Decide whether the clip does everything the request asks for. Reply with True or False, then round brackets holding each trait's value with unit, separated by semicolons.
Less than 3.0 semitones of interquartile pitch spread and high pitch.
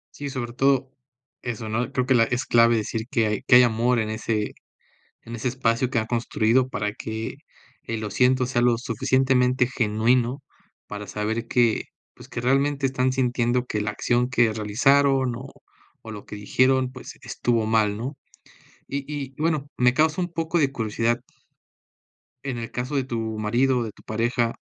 False (2.6 semitones; 120 Hz)